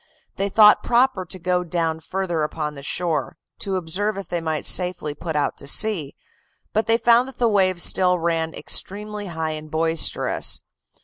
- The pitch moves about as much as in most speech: Yes, average, 4.0 semitones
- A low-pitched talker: No, medium, 180 Hz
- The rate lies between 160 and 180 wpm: Yes, average, 175 wpm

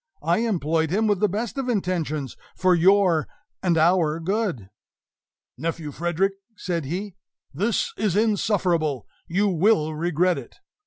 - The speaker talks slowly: Yes, slow, 130 wpm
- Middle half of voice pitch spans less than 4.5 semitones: Yes, average, 4.1 semitones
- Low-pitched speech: No, medium, 180 Hz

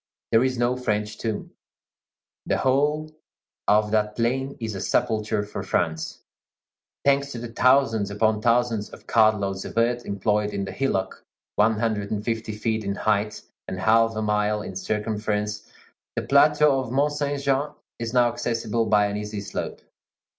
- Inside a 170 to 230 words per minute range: No, average, 160 wpm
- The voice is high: No, low, 110 Hz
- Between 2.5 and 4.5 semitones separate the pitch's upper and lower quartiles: Yes, average, 2.8 semitones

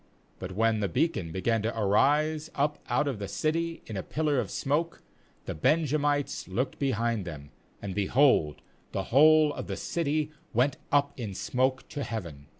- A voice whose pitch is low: Yes, low, 130 Hz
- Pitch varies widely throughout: Yes, wide, 6.6 semitones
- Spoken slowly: No, average, 165 wpm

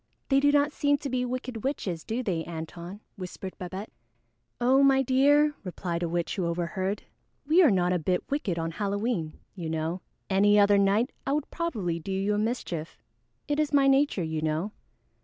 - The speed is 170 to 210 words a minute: Yes, average, 185 wpm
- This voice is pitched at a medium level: No, high, 200 Hz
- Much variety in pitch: Yes, wide, 7.5 semitones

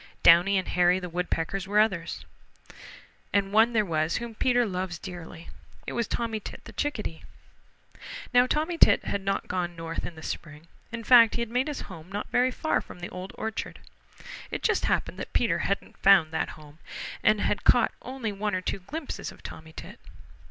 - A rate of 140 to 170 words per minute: No, average, 190 wpm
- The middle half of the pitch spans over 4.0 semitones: Yes, average, 5.1 semitones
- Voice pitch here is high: Yes, high, 195 Hz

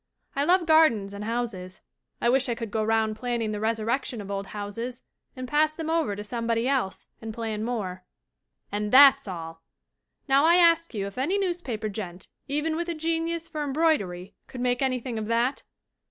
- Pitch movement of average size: No, wide, 6.0 semitones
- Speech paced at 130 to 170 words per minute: No, average, 185 wpm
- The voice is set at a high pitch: Yes, high, 235 Hz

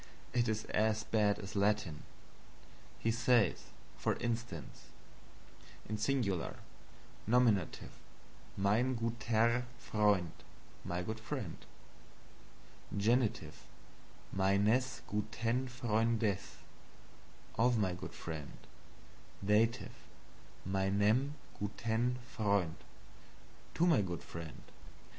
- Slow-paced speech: Yes, slow, 80 wpm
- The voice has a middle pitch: No, low, 110 Hz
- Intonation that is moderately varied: Yes, average, 3.0 semitones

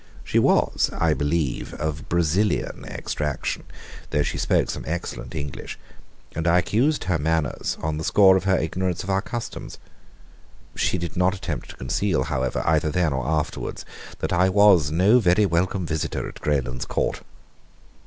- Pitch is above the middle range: No, very low, 85 Hz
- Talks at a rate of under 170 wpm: Yes, average, 155 wpm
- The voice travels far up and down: No, average, 4.0 semitones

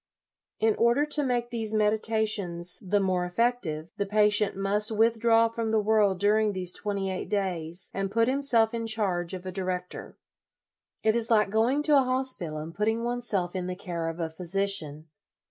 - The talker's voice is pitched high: Yes, high, 210 Hz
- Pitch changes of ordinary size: Yes, average, 3.9 semitones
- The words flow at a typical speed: Yes, average, 180 wpm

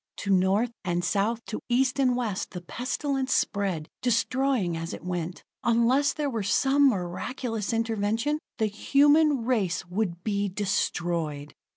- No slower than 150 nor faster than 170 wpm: No, average, 140 wpm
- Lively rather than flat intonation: Yes, wide, 5.7 semitones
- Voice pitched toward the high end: Yes, high, 220 Hz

